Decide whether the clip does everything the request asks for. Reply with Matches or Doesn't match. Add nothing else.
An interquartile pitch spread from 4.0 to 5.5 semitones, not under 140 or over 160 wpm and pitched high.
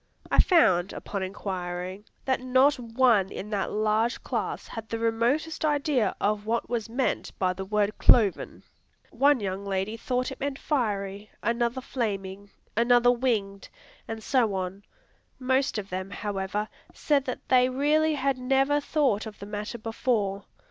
Matches